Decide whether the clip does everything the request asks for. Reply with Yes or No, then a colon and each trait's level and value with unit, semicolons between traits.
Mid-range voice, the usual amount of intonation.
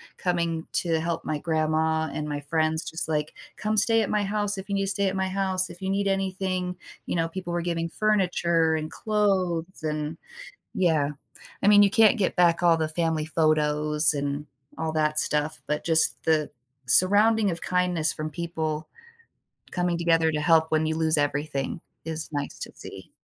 Yes: medium, 165 Hz; average, 3.3 semitones